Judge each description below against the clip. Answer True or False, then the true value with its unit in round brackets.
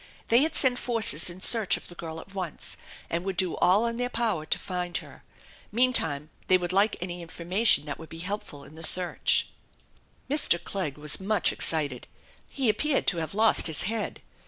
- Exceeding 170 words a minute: True (190 wpm)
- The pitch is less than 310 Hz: True (185 Hz)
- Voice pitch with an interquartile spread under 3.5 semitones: False (5.2 semitones)